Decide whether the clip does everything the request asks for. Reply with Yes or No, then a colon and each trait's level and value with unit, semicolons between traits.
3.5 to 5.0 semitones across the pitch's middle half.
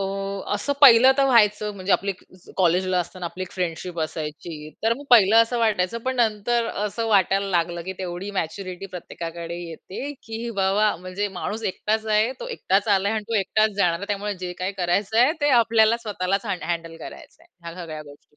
Yes: average, 3.8 semitones